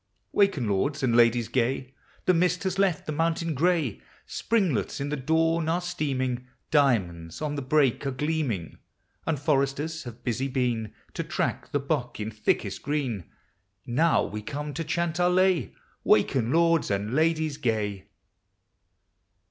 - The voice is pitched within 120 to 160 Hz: Yes, medium, 140 Hz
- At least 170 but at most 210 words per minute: No, average, 150 wpm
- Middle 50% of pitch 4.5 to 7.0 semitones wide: Yes, average, 5.2 semitones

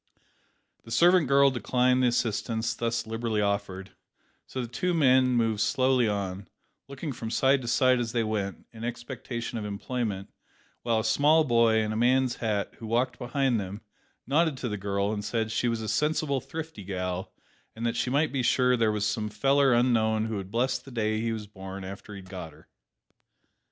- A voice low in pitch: Yes, low, 115 Hz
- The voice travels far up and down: No, average, 3.3 semitones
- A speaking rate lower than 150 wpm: No, average, 190 wpm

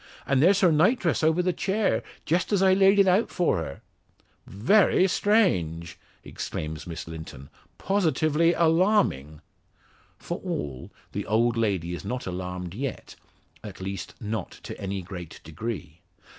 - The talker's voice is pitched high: No, low, 120 Hz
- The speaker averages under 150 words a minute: Yes, average, 140 wpm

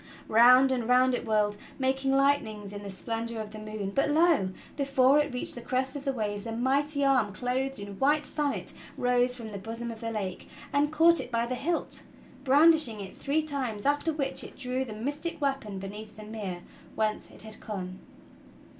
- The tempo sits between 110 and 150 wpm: No, average, 200 wpm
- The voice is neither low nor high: No, very high, 250 Hz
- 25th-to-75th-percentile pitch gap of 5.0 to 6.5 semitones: No, average, 4.5 semitones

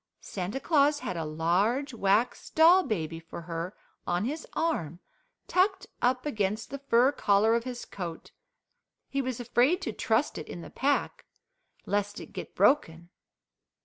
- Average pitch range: No, wide, 7.9 semitones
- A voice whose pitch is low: No, high, 225 Hz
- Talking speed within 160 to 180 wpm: No, average, 150 wpm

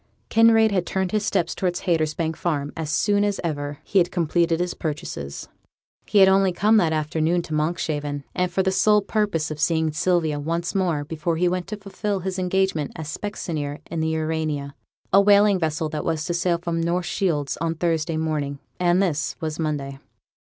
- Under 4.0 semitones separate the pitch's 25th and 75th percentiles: Yes, average, 3.4 semitones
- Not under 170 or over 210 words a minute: Yes, average, 190 wpm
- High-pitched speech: No, medium, 170 Hz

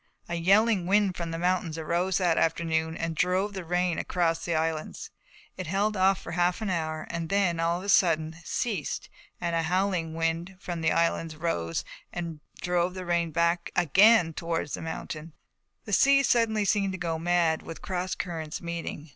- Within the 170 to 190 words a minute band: Yes, average, 180 wpm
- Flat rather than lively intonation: Yes, narrow, 2.3 semitones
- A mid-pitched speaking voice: Yes, medium, 170 Hz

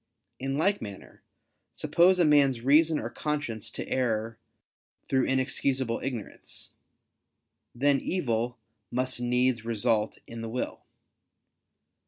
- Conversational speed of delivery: No, slow, 110 wpm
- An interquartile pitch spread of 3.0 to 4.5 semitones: Yes, average, 3.4 semitones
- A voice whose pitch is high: No, low, 130 Hz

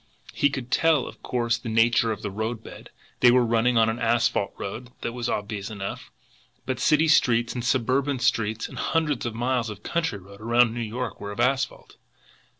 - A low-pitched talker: Yes, low, 120 Hz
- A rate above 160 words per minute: Yes, average, 190 wpm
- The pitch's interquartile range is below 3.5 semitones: Yes, narrow, 2.4 semitones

